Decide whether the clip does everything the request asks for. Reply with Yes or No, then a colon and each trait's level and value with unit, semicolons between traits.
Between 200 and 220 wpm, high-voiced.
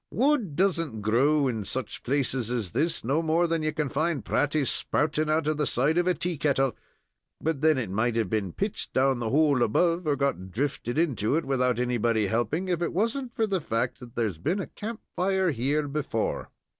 No: fast, 205 wpm; medium, 145 Hz